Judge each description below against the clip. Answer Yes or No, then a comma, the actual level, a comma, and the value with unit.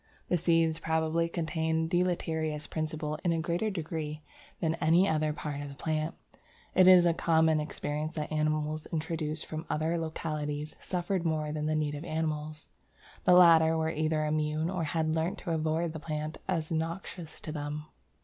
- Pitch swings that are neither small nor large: No, narrow, 1.4 semitones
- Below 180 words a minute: Yes, average, 170 wpm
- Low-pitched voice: No, medium, 160 Hz